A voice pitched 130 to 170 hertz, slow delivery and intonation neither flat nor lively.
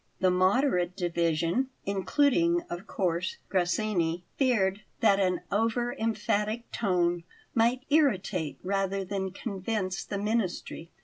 No: high, 195 Hz; slow, 110 wpm; average, 4.0 semitones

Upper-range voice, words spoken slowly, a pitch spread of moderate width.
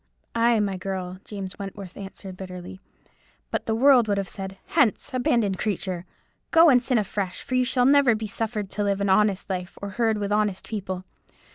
No: high, 205 Hz; average, 190 wpm; average, 3.2 semitones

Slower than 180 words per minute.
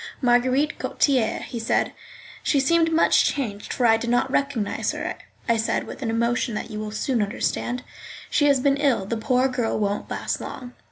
No: average, 185 wpm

